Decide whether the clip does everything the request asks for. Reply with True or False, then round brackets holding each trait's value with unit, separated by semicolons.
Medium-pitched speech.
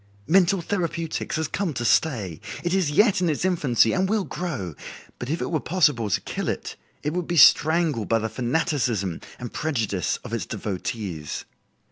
True (150 Hz)